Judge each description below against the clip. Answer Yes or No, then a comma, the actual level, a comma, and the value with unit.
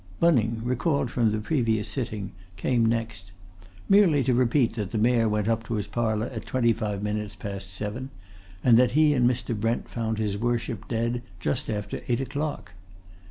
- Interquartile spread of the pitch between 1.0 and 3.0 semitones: Yes, average, 2.7 semitones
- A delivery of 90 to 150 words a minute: No, average, 175 wpm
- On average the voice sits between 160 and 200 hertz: No, low, 115 Hz